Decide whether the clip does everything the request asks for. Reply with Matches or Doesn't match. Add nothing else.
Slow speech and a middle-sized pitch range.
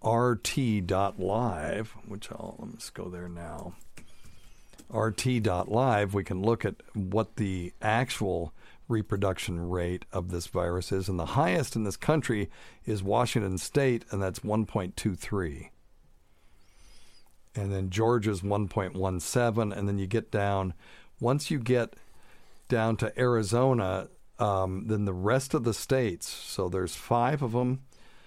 Matches